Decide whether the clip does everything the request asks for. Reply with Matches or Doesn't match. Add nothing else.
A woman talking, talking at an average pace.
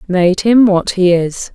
Matches